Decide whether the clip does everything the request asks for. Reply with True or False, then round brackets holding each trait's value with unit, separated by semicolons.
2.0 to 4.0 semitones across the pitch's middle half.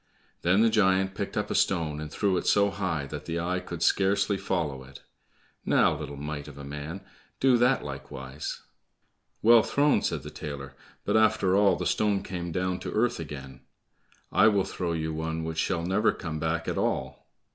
False (4.6 semitones)